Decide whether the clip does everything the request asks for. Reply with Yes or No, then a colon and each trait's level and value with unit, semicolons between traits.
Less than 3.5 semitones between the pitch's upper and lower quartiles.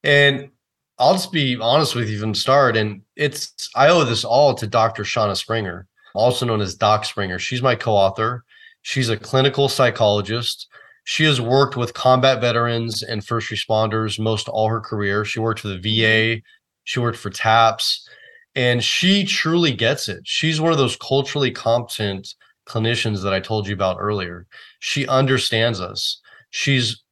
No: average, 3.8 semitones